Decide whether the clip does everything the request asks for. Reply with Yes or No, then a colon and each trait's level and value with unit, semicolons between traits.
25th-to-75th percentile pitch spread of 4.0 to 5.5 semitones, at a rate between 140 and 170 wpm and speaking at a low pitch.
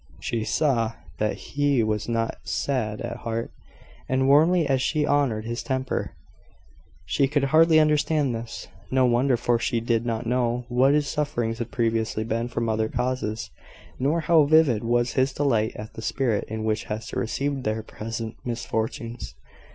No: average, 3.5 semitones; average, 160 wpm; low, 120 Hz